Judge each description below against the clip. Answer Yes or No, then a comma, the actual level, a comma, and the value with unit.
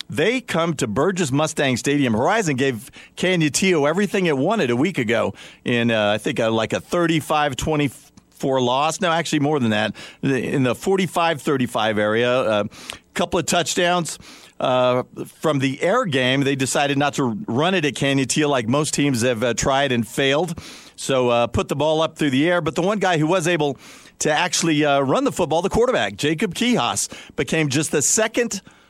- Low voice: No, medium, 150 Hz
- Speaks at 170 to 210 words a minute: Yes, average, 190 wpm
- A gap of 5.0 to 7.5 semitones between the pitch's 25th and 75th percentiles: No, average, 4.6 semitones